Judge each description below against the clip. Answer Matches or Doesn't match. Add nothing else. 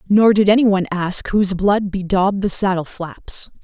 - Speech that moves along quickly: Doesn't match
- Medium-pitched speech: Doesn't match